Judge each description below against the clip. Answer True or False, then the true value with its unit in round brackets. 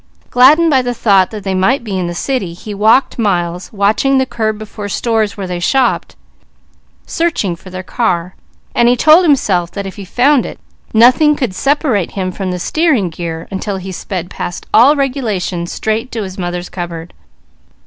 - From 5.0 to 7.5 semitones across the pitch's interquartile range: True (5.5 semitones)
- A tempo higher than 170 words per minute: True (180 wpm)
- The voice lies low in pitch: False (205 Hz)